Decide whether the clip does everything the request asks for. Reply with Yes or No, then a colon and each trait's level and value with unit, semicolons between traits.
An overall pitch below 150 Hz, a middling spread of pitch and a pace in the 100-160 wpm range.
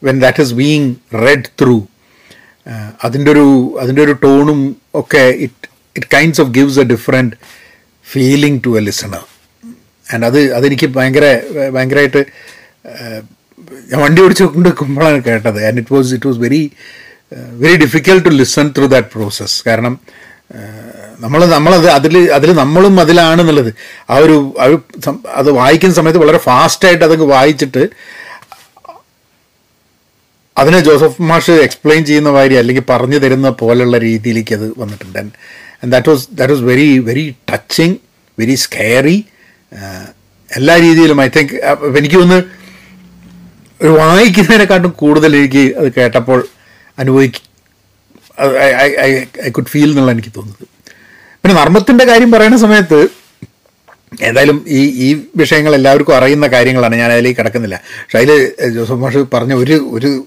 Yes: medium, 140 Hz; average, 4.3 semitones; average, 120 wpm